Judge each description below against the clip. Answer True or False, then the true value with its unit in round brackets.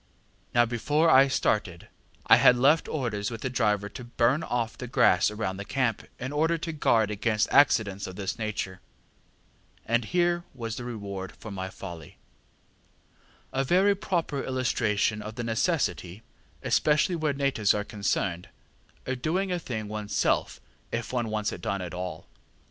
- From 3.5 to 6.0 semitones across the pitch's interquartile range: True (4.9 semitones)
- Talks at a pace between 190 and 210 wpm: False (160 wpm)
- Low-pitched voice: True (115 Hz)